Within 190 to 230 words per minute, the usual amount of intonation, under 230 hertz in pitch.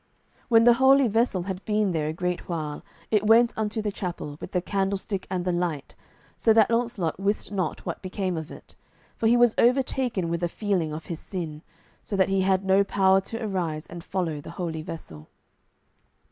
Yes: average, 195 wpm; average, 4.1 semitones; high, 190 Hz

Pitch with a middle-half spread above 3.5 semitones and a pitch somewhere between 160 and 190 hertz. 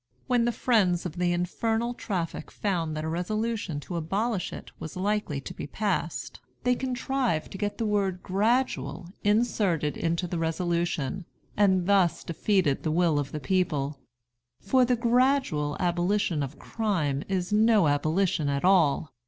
Yes: average, 4.8 semitones; medium, 185 Hz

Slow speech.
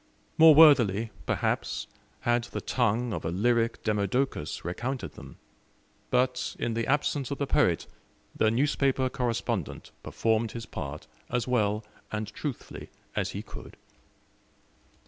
Yes: slow, 125 wpm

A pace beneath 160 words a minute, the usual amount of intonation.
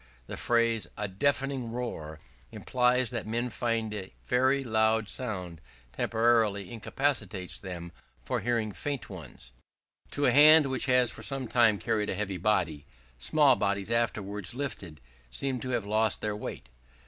Yes: average, 150 wpm; average, 4.0 semitones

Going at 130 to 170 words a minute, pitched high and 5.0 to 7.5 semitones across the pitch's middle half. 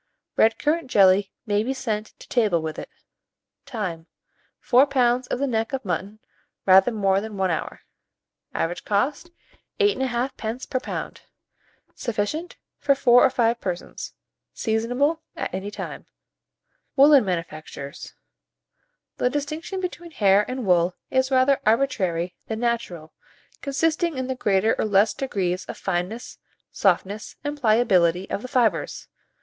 Yes: slow, 135 wpm; high, 225 Hz; wide, 5.5 semitones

